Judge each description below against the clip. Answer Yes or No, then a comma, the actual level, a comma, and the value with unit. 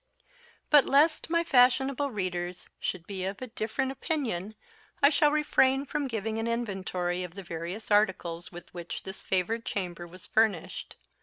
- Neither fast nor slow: Yes, average, 155 wpm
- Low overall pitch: No, high, 215 Hz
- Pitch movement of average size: No, wide, 6.7 semitones